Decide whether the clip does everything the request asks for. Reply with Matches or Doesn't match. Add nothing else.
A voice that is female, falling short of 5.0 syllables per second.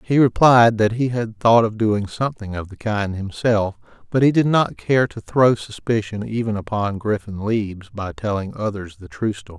Doesn't match